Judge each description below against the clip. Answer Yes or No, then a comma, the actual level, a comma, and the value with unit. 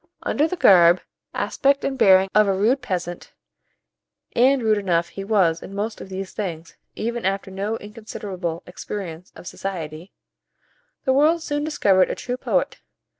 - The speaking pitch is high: Yes, high, 195 Hz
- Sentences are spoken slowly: No, average, 155 wpm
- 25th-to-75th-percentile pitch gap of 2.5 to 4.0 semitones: No, average, 4.6 semitones